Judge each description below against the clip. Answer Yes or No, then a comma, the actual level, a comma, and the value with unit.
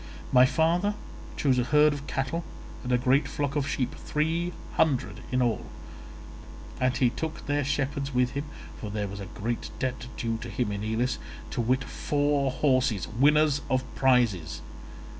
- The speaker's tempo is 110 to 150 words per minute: No, average, 160 wpm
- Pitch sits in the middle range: No, low, 130 Hz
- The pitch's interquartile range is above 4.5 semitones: No, average, 3.3 semitones